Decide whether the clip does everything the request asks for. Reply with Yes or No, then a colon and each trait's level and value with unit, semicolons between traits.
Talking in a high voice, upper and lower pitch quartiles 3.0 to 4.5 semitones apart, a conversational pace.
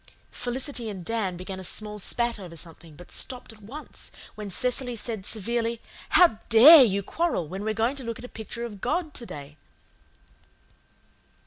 Yes: high, 225 Hz; average, 4.2 semitones; average, 180 wpm